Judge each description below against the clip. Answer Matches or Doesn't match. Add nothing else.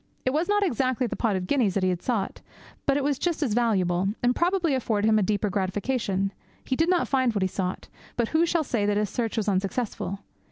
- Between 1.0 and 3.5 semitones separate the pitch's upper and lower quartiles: Doesn't match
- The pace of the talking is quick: Matches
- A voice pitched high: Matches